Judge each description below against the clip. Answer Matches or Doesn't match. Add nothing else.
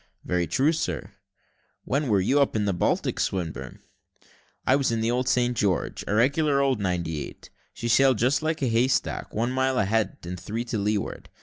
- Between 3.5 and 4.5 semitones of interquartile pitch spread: Doesn't match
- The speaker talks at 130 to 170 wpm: Doesn't match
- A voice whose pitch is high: Doesn't match